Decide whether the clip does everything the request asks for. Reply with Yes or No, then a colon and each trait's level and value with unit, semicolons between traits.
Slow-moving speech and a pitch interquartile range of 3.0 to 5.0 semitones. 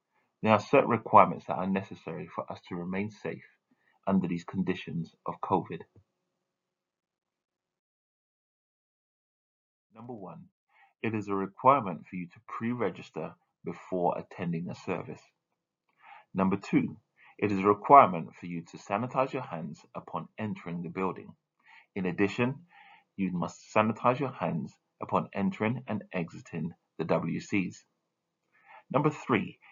Yes: slow, 125 wpm; average, 3.5 semitones